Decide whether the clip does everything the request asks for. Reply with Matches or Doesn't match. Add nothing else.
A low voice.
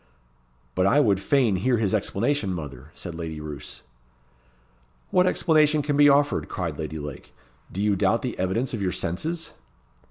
Matches